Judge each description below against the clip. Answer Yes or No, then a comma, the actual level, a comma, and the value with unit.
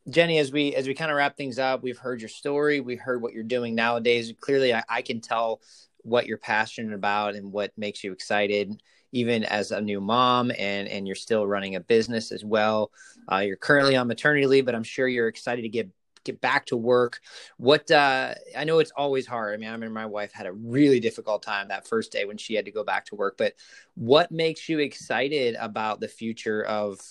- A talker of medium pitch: No, low, 115 Hz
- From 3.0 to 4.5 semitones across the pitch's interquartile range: Yes, average, 4.0 semitones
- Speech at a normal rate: No, fast, 230 wpm